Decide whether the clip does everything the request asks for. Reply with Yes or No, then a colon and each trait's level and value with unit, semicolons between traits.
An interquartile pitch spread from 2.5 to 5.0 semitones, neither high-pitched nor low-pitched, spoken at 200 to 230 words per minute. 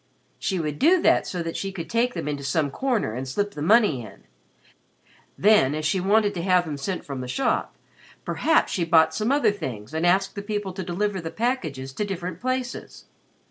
No: wide, 5.6 semitones; medium, 180 Hz; fast, 205 wpm